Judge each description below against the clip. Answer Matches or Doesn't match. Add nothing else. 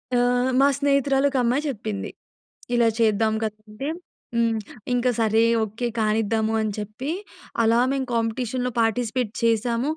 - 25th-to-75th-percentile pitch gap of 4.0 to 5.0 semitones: Doesn't match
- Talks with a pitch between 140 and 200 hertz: Doesn't match